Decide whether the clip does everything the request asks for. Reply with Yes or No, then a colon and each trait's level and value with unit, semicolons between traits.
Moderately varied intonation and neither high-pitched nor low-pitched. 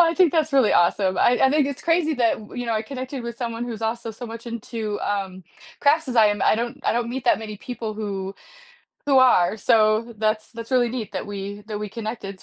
No: average, 3.1 semitones; high, 230 Hz